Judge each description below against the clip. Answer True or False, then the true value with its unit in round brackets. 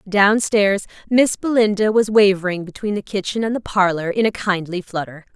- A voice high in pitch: True (200 Hz)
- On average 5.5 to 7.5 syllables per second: False (5.1 syllables/s)